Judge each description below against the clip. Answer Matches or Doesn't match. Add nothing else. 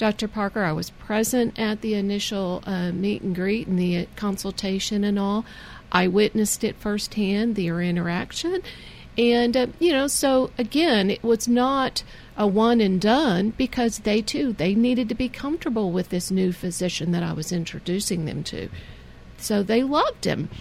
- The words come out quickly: Doesn't match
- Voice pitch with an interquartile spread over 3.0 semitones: Matches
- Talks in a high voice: Matches